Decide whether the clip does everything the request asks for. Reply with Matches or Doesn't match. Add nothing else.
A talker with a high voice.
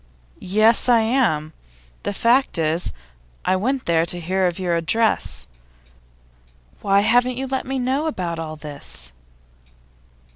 Matches